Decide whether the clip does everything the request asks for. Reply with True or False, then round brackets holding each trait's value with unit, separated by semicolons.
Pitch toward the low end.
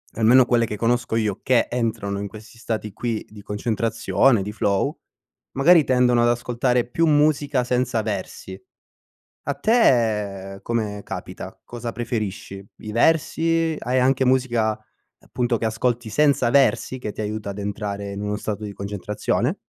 True (115 Hz)